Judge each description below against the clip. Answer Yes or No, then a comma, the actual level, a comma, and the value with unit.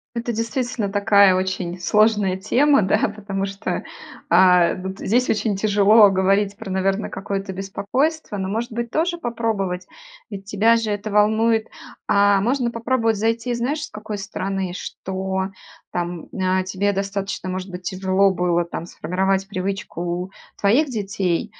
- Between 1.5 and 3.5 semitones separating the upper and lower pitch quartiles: Yes, average, 2.9 semitones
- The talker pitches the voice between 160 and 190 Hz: No, high, 200 Hz